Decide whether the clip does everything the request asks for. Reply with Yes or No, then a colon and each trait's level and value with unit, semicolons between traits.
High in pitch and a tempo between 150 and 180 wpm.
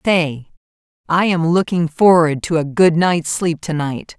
No: medium, 165 Hz; average, 170 wpm